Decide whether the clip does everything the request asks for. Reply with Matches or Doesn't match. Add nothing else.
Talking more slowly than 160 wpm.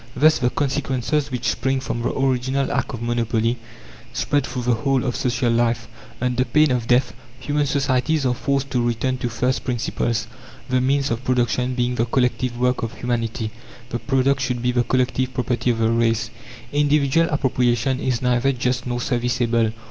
Doesn't match